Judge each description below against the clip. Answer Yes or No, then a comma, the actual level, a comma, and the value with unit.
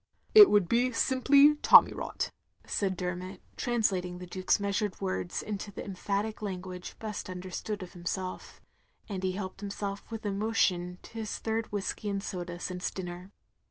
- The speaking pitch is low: No, high, 195 Hz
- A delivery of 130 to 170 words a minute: Yes, average, 165 wpm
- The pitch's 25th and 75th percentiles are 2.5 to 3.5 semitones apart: Yes, average, 2.9 semitones